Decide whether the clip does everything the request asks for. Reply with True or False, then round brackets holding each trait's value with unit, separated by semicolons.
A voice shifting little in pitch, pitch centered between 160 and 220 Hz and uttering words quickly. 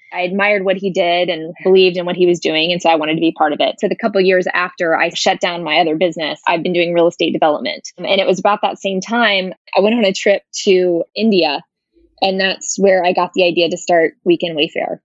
True (2.2 semitones; 185 Hz; 255 wpm)